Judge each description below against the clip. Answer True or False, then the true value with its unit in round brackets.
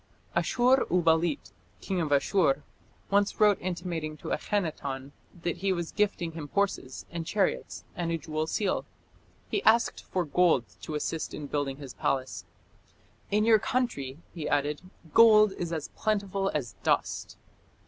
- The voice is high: False (170 Hz)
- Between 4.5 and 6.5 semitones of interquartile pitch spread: True (5.1 semitones)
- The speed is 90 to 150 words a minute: True (145 wpm)